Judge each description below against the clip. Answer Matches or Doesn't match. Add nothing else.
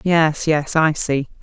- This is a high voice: Doesn't match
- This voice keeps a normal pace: Matches